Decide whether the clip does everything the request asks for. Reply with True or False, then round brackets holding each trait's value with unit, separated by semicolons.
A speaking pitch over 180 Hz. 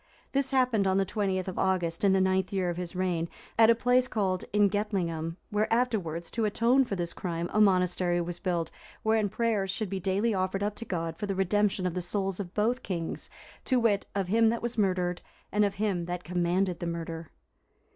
True (190 Hz)